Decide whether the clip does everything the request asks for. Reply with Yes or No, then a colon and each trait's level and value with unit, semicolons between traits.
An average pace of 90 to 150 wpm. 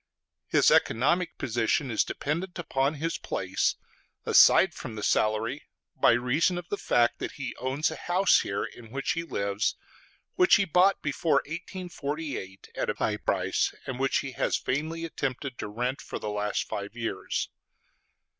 No: average, 160 wpm